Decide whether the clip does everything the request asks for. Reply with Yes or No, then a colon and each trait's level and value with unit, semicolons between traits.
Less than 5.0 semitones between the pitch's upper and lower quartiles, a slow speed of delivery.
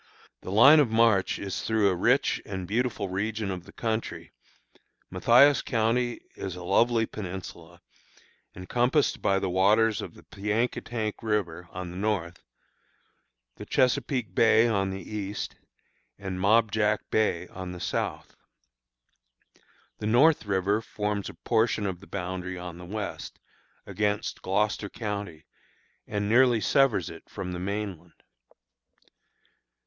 Yes: average, 3.3 semitones; slow, 130 wpm